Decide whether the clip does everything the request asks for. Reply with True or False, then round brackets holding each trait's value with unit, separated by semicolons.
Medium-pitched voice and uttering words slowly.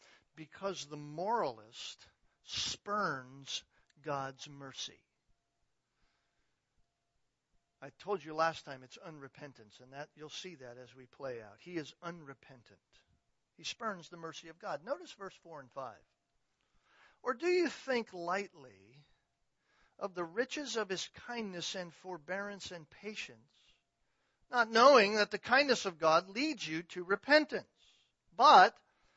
True (175 Hz; 130 wpm)